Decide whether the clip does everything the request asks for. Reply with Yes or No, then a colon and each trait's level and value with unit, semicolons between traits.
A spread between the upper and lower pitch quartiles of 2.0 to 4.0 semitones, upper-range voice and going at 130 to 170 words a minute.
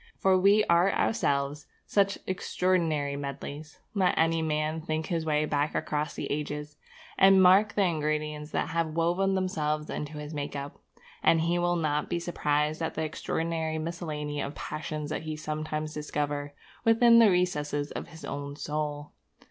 No: narrow, 2.6 semitones; medium, 155 Hz; average, 160 wpm